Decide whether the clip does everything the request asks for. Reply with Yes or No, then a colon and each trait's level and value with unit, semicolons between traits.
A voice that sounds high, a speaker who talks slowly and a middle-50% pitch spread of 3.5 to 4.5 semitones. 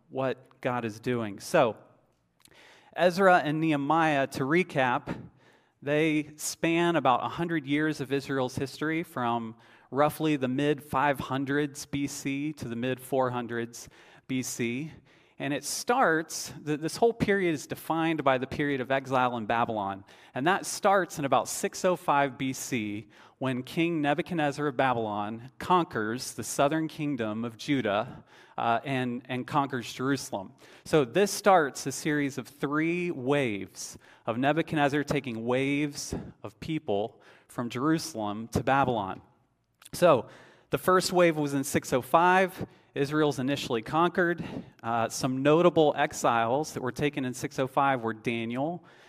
No: medium, 140 Hz; slow, 130 wpm; average, 4.0 semitones